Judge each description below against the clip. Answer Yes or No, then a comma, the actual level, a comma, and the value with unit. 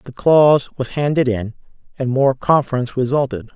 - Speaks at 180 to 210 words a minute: No, average, 150 wpm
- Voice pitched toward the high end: No, low, 130 Hz